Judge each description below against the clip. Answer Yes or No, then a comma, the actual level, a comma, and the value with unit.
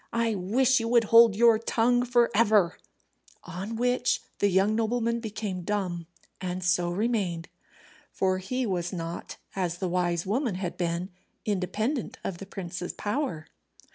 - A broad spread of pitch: No, average, 4.4 semitones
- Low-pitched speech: No, high, 200 Hz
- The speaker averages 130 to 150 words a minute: Yes, average, 145 wpm